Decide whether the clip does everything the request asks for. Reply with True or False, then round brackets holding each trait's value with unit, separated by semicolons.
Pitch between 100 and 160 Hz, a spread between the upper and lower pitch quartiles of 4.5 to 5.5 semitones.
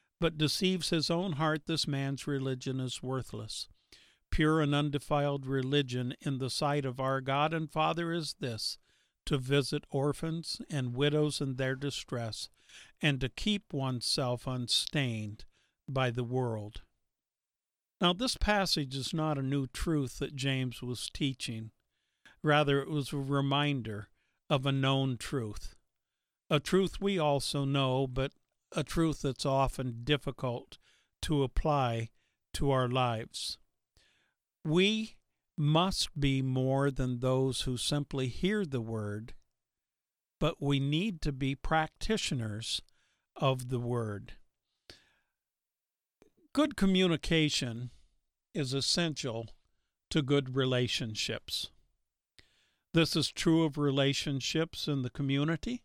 False (140 Hz; 3.5 semitones)